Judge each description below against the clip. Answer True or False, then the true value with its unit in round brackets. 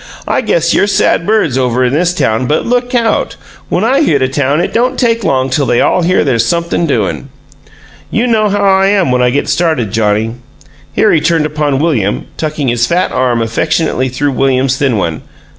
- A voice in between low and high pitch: True (145 Hz)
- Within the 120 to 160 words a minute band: False (200 wpm)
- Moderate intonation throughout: False (6.6 semitones)